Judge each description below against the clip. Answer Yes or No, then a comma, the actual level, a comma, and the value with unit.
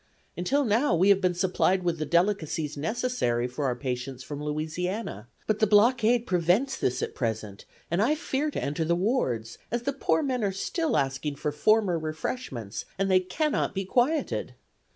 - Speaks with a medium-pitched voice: Yes, medium, 180 Hz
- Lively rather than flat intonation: Yes, wide, 7.7 semitones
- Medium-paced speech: Yes, average, 175 wpm